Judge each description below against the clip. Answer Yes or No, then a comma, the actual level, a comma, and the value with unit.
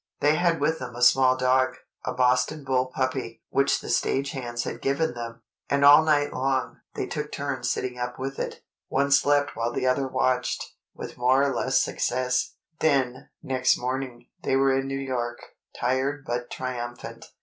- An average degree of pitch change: No, narrow, 1.7 semitones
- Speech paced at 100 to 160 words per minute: No, average, 170 wpm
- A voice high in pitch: No, low, 130 Hz